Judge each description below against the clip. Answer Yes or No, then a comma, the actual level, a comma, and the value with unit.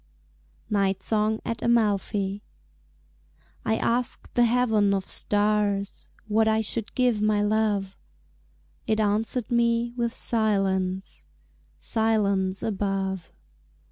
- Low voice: No, high, 210 Hz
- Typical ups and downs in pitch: No, narrow, 2.2 semitones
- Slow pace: Yes, slow, 100 wpm